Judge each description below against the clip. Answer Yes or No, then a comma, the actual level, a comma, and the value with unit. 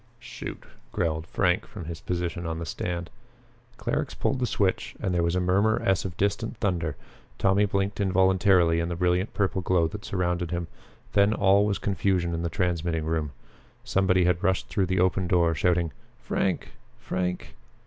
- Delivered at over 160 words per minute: Yes, average, 170 wpm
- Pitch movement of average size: No, narrow, 2.1 semitones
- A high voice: No, very low, 90 Hz